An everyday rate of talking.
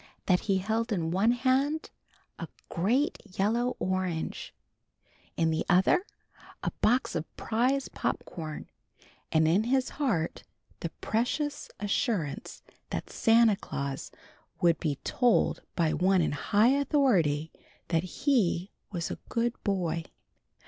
No: slow, 125 wpm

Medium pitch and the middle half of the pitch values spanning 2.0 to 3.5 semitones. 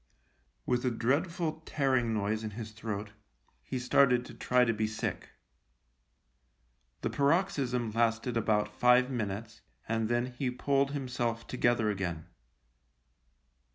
No: low, 120 Hz; average, 2.7 semitones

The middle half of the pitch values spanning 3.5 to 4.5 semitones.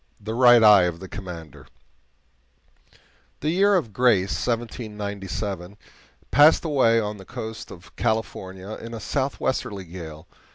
Yes: average, 4.2 semitones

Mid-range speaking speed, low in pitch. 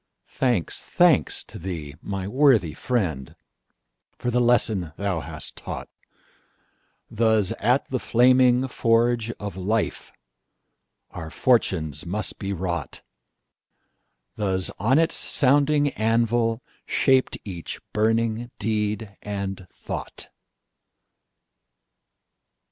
No: slow, 80 wpm; low, 110 Hz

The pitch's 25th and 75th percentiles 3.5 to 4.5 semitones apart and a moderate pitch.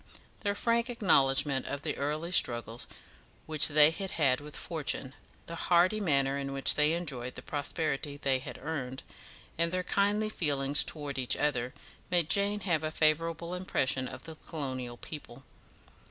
Yes: average, 4.0 semitones; medium, 150 Hz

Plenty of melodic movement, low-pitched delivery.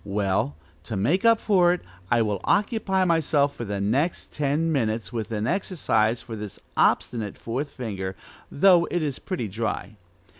Yes: wide, 8.1 semitones; low, 120 Hz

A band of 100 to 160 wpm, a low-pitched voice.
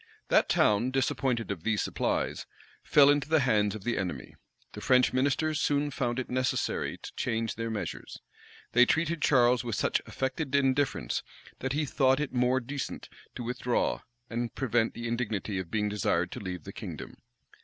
No: average, 170 wpm; low, 125 Hz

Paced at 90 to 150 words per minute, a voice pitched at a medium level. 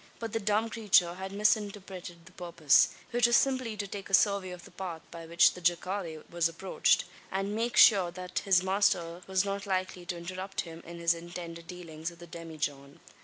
No: average, 195 wpm; medium, 180 Hz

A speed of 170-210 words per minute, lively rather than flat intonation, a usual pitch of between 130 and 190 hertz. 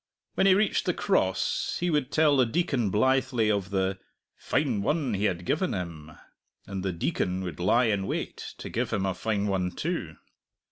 No: average, 185 wpm; wide, 6.1 semitones; low, 105 Hz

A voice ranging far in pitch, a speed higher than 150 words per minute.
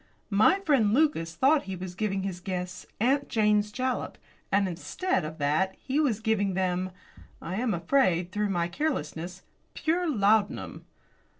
No: wide, 6.1 semitones; average, 145 wpm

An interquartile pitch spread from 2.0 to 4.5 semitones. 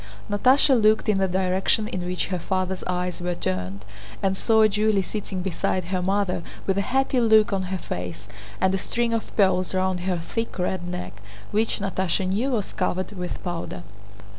Yes: average, 2.7 semitones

